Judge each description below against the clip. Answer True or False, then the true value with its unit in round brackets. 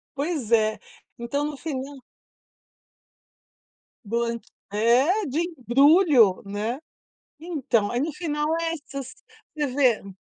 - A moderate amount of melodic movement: True (4.4 semitones)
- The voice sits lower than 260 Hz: False (270 Hz)